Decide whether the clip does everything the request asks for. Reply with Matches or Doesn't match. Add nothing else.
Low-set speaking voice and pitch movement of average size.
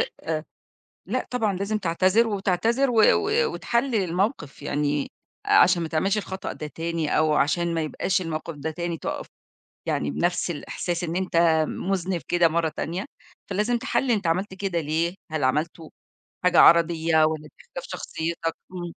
Doesn't match